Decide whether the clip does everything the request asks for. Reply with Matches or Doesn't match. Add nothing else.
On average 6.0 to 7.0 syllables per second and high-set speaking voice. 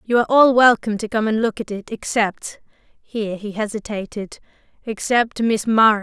Doesn't match